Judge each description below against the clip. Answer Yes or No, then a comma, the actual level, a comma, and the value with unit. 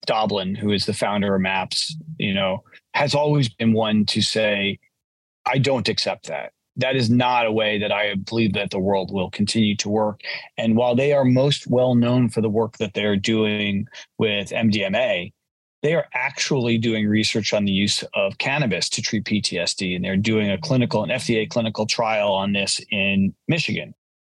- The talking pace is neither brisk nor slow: Yes, average, 185 wpm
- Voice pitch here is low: Yes, low, 110 Hz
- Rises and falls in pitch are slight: No, average, 3.0 semitones